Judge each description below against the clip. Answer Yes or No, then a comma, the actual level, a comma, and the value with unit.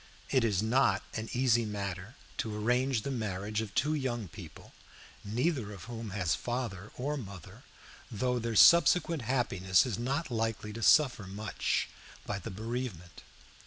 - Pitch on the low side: Yes, low, 115 Hz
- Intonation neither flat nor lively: Yes, average, 3.8 semitones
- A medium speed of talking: Yes, average, 150 wpm